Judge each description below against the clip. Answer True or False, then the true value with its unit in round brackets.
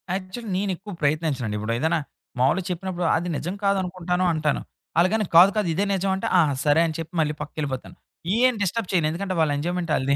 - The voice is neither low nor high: True (175 Hz)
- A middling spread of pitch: True (3.8 semitones)